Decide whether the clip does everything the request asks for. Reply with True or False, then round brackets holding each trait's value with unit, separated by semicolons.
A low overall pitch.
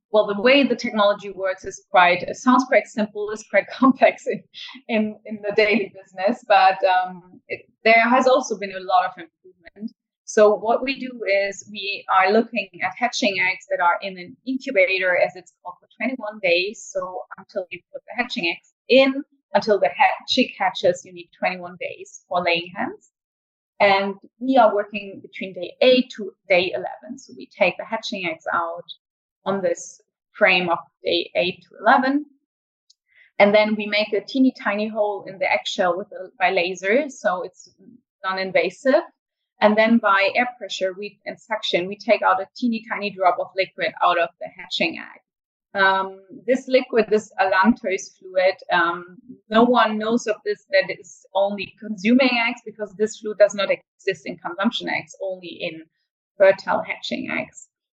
False (210 Hz)